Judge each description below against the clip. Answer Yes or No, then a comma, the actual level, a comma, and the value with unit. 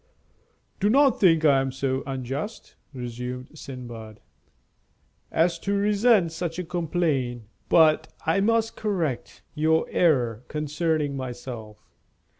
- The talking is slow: Yes, slow, 110 wpm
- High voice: No, medium, 155 Hz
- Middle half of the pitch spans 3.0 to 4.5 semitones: No, wide, 5.6 semitones